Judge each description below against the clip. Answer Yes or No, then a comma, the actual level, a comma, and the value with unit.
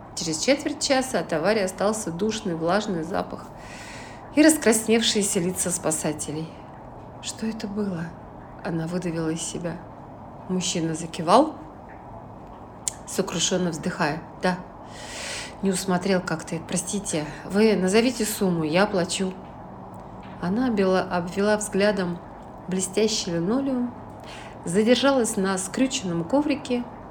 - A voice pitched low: No, high, 190 Hz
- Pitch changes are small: No, average, 4.4 semitones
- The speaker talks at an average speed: No, slow, 95 wpm